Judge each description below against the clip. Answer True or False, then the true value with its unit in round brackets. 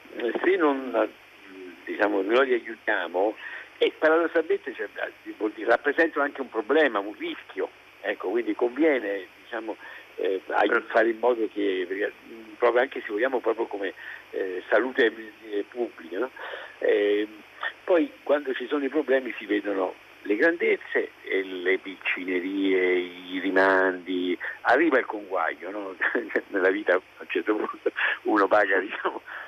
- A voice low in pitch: False (370 Hz)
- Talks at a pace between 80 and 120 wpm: False (130 wpm)